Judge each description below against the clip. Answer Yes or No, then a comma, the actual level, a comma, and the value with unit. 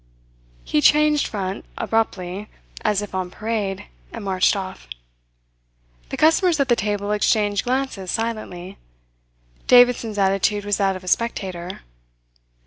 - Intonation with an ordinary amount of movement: Yes, average, 3.3 semitones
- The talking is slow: Yes, slow, 125 wpm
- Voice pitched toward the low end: No, high, 205 Hz